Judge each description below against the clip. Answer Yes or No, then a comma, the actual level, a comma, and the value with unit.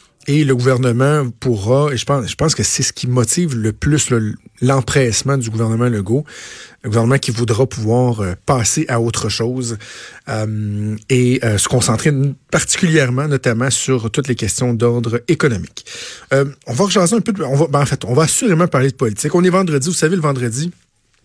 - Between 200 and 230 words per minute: No, average, 190 wpm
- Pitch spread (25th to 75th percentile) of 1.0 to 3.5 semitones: No, average, 3.9 semitones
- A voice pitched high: No, low, 130 Hz